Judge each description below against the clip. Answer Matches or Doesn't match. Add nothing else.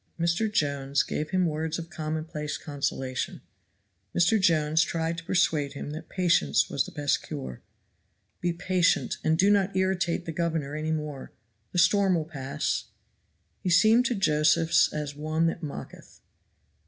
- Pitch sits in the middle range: Matches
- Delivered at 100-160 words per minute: Matches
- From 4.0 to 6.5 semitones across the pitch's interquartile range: Doesn't match